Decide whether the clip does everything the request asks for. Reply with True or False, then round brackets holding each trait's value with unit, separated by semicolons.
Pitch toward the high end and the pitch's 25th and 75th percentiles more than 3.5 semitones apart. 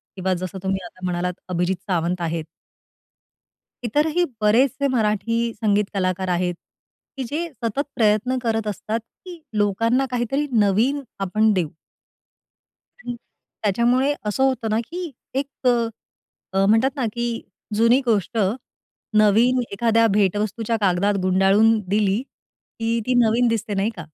True (220 Hz; 3.9 semitones)